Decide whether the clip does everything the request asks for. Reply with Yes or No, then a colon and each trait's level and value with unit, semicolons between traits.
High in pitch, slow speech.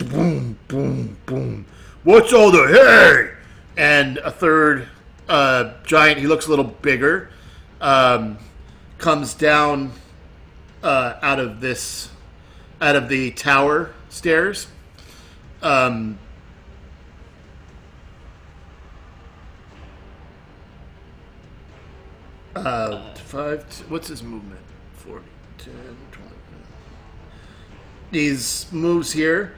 No: low, 100 Hz; slow, 80 wpm